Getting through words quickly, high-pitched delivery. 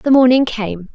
No: average, 190 wpm; high, 240 Hz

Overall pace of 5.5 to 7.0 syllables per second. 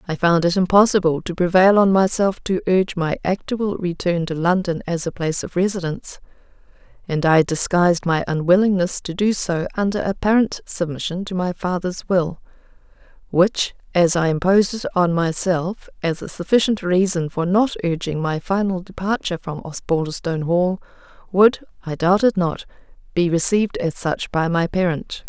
No: 5.1 syllables/s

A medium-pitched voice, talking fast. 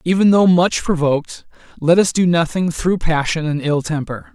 No: medium, 165 Hz; average, 180 wpm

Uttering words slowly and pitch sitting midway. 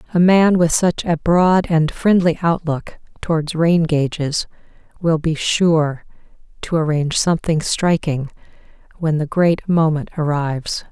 Yes: slow, 130 wpm; medium, 160 Hz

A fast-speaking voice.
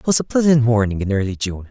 Yes: fast, 280 wpm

